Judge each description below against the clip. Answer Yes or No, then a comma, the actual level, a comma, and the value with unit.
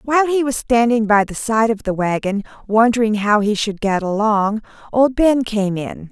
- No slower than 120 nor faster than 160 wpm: No, average, 195 wpm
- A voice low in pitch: No, high, 220 Hz